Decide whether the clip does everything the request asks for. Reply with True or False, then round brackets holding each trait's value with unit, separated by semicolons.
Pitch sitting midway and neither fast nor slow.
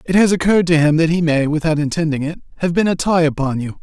False (160 Hz; 265 wpm)